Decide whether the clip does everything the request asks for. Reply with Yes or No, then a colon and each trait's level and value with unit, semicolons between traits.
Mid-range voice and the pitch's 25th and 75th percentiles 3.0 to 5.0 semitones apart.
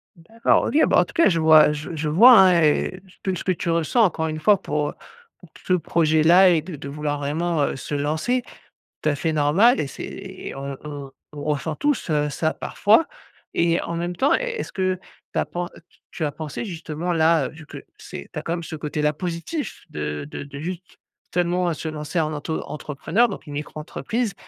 Yes: medium, 160 Hz; average, 3.4 semitones